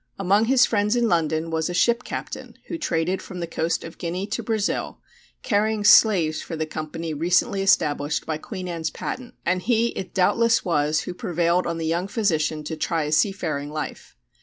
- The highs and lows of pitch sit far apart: No, average, 4.4 semitones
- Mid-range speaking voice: Yes, medium, 175 Hz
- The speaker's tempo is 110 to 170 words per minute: No, average, 185 wpm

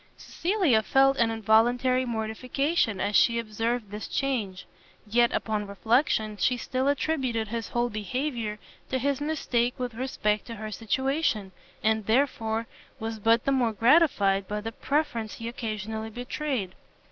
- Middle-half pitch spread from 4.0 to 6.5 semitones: No, average, 3.2 semitones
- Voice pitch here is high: Yes, high, 230 Hz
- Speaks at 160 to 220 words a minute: No, average, 140 wpm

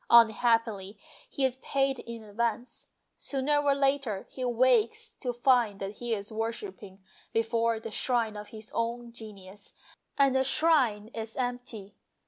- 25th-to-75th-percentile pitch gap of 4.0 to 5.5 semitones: No, average, 3.1 semitones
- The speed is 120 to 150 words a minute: Yes, average, 140 wpm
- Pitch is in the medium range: No, high, 230 Hz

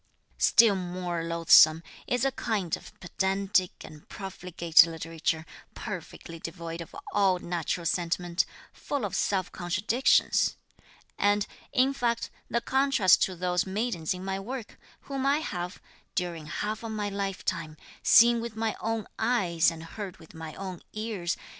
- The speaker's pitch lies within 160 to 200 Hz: Yes, medium, 185 Hz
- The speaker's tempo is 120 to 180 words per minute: Yes, average, 140 wpm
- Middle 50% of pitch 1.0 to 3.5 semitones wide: No, average, 4.4 semitones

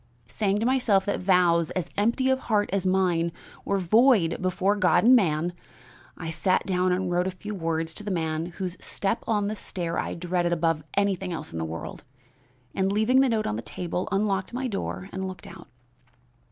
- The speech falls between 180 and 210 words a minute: Yes, average, 195 wpm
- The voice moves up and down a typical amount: Yes, average, 3.4 semitones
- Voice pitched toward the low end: No, medium, 185 Hz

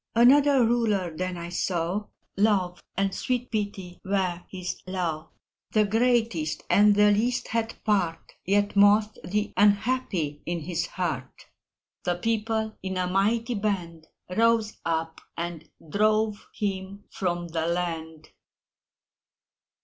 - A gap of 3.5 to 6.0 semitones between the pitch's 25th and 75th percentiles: Yes, average, 3.8 semitones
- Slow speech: Yes, slow, 120 wpm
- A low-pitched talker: No, high, 195 Hz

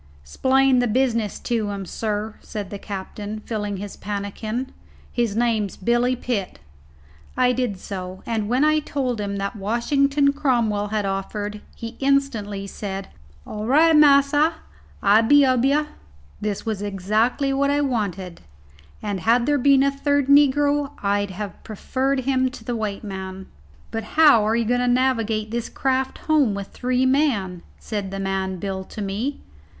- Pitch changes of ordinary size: Yes, average, 4.8 semitones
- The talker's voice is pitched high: Yes, high, 225 Hz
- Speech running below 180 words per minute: Yes, average, 160 wpm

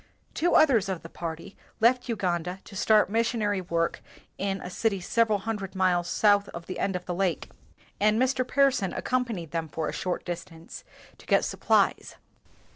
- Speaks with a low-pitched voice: No, high, 195 Hz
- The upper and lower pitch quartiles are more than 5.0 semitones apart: No, average, 4.3 semitones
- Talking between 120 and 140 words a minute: No, average, 170 wpm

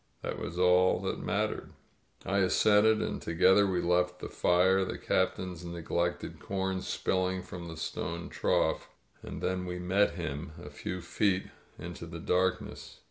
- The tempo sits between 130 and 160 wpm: Yes, average, 155 wpm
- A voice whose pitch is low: Yes, very low, 90 Hz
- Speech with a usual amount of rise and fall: No, narrow, 1.4 semitones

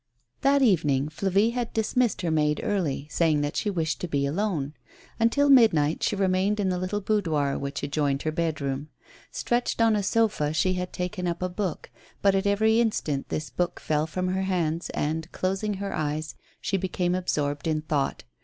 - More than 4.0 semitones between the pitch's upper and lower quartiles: Yes, average, 5.1 semitones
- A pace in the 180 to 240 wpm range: Yes, average, 185 wpm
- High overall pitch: No, medium, 180 Hz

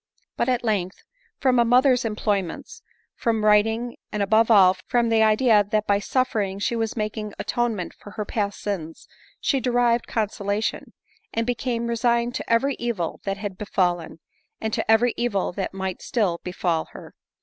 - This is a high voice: Yes, high, 220 Hz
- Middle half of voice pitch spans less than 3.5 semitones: Yes, average, 2.8 semitones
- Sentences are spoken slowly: No, average, 160 wpm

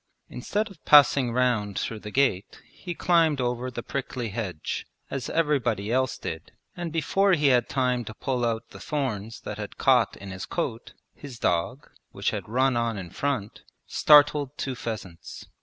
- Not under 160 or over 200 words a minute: Yes, average, 175 wpm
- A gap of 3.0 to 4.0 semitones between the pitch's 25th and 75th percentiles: No, average, 4.4 semitones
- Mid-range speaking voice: No, low, 125 Hz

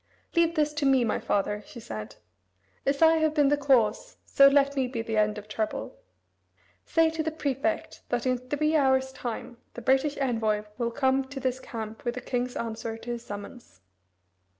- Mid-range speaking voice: No, very high, 255 Hz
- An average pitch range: Yes, average, 3.9 semitones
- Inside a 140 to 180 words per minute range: No, average, 190 wpm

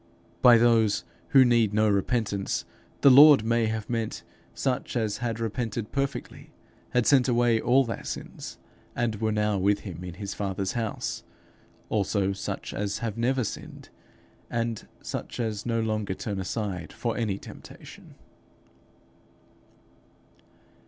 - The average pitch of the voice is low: Yes, low, 110 Hz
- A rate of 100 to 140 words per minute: Yes, slow, 135 wpm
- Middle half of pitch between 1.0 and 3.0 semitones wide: Yes, average, 2.7 semitones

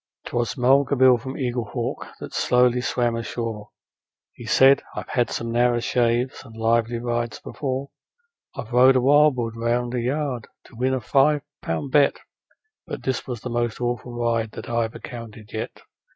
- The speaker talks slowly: No, average, 165 wpm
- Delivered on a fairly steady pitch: Yes, narrow, 1.9 semitones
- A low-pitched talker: Yes, low, 120 Hz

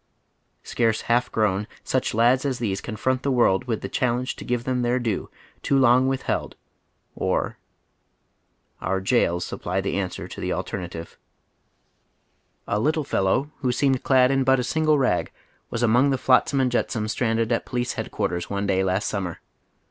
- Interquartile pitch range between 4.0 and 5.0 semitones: Yes, average, 4.6 semitones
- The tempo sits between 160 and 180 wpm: Yes, average, 170 wpm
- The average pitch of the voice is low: Yes, low, 120 Hz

